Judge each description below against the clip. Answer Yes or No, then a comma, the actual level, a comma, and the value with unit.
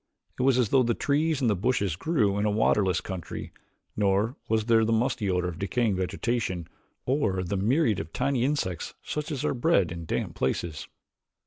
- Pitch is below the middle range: Yes, low, 110 Hz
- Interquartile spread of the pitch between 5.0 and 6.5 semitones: Yes, average, 5.3 semitones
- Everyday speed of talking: Yes, average, 190 wpm